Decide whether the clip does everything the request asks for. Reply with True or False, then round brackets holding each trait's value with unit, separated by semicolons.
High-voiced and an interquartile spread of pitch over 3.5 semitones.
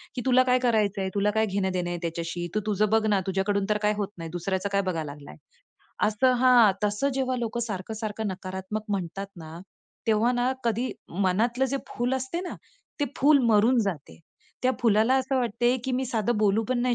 True (215 Hz; 4.2 semitones)